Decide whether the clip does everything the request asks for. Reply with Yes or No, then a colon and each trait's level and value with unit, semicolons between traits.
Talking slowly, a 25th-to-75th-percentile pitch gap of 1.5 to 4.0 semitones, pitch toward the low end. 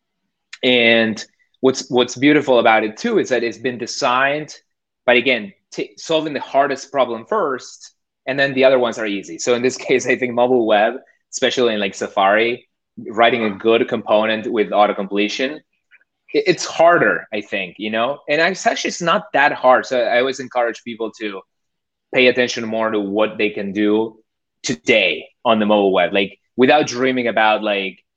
No: average, 175 wpm; average, 3.5 semitones; low, 120 Hz